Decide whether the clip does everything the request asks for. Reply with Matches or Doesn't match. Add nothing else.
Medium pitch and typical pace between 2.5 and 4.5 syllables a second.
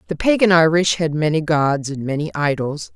Doesn't match